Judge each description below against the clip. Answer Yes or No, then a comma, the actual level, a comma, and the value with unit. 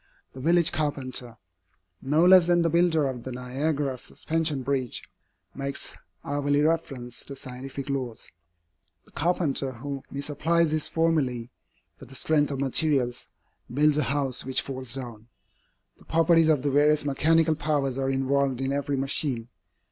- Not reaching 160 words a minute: Yes, average, 145 wpm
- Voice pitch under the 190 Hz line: Yes, medium, 140 Hz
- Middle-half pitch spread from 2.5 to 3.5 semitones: Yes, average, 2.9 semitones